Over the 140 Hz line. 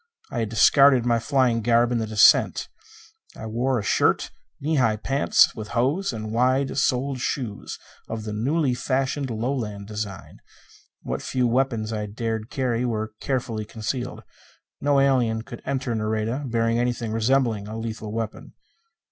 No: low, 115 Hz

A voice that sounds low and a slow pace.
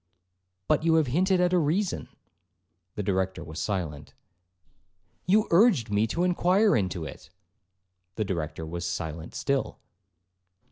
Yes: low, 115 Hz; slow, 130 wpm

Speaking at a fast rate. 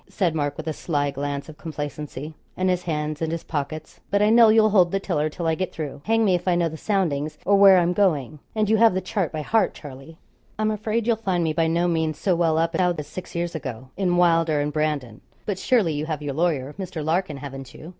Yes: fast, 245 wpm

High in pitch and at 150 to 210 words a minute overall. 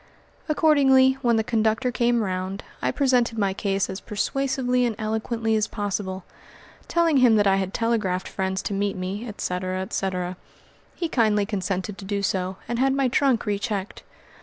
Yes: high, 215 Hz; average, 165 wpm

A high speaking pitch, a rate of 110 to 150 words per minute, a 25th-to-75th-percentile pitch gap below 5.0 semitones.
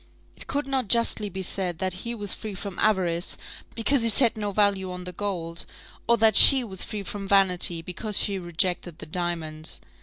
No: high, 195 Hz; average, 190 wpm; average, 3.4 semitones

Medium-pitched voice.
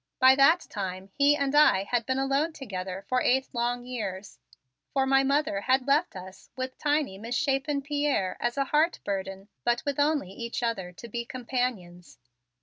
No: very high, 255 Hz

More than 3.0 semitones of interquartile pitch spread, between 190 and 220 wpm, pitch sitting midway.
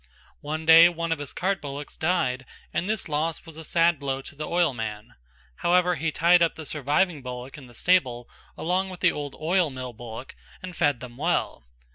Yes: average, 4.6 semitones; average, 195 wpm; medium, 155 Hz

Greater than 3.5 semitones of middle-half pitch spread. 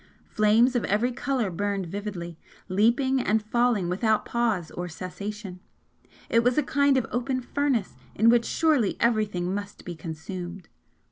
Yes: average, 4.7 semitones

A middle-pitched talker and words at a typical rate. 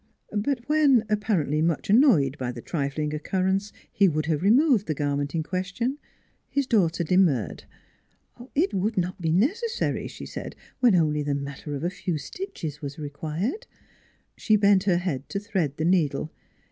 Yes: medium, 180 Hz; average, 160 wpm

